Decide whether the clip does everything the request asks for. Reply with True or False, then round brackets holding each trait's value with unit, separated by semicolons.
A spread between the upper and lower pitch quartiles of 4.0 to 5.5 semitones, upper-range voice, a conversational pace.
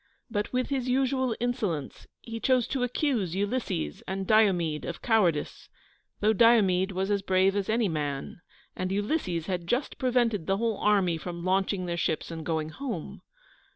True (5.2 semitones; 195 Hz; 160 wpm)